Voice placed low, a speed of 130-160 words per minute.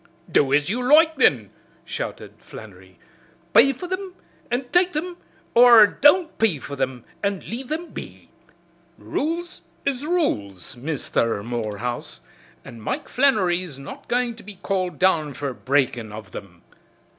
No: medium, 185 Hz; average, 140 wpm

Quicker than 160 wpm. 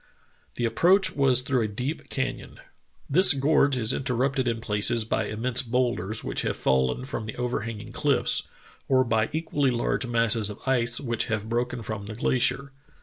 Yes: average, 170 wpm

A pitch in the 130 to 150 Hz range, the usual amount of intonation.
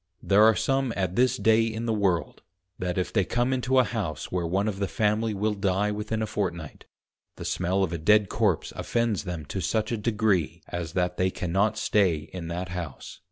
No: low, 100 Hz; average, 3.5 semitones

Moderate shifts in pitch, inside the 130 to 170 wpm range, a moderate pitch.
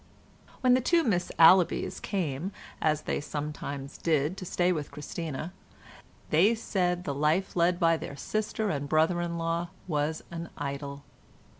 Yes: average, 3.5 semitones; average, 150 wpm; medium, 165 Hz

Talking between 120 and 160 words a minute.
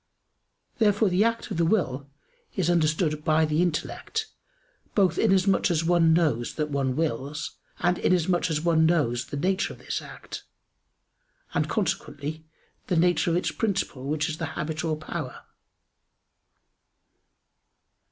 Yes: average, 140 wpm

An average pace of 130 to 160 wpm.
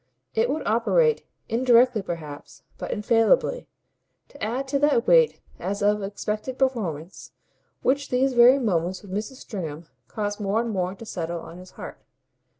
Yes: average, 150 wpm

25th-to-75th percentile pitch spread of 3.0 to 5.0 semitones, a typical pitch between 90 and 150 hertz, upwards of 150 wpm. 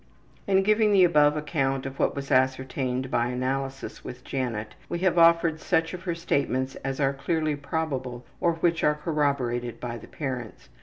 Yes: average, 4.0 semitones; medium, 140 Hz; average, 170 wpm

